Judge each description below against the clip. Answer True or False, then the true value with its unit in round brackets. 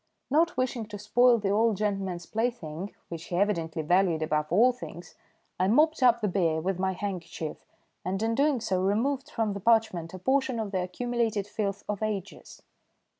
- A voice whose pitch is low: False (205 Hz)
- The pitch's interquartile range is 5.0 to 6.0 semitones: False (4.4 semitones)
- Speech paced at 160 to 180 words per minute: True (175 wpm)